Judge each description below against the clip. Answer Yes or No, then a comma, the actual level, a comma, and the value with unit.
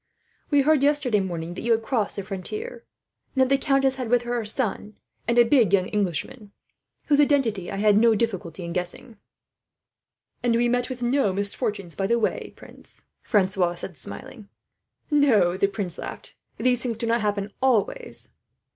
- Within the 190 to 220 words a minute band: No, average, 175 wpm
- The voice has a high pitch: Yes, high, 225 Hz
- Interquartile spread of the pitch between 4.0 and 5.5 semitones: Yes, average, 4.7 semitones